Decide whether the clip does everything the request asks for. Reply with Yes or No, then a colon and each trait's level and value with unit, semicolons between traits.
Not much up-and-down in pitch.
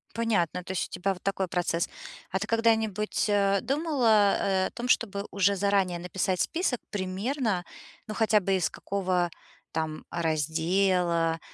No: average, 3.2 semitones